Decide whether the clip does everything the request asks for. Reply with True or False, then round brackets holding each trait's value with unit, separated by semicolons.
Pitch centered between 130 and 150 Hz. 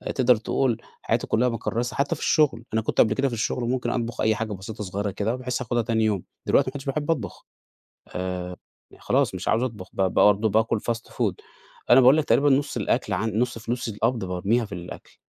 False (115 Hz)